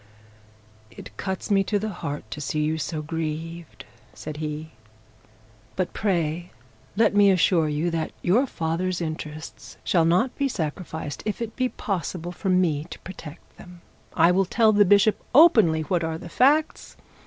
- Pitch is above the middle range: No, medium, 175 Hz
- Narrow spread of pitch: No, average, 4.1 semitones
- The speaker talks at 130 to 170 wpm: Yes, average, 160 wpm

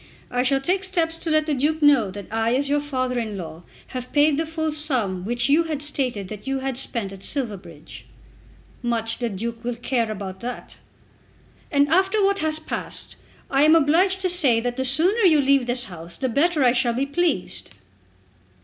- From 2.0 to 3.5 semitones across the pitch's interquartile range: No, average, 5.1 semitones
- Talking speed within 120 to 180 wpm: No, average, 195 wpm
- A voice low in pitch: No, very high, 265 Hz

